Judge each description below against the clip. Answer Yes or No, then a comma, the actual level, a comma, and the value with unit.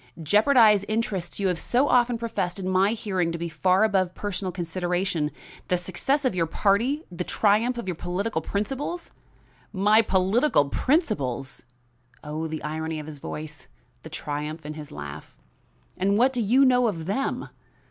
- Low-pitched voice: No, high, 190 Hz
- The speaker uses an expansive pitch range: Yes, wide, 5.7 semitones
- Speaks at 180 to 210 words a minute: No, average, 160 wpm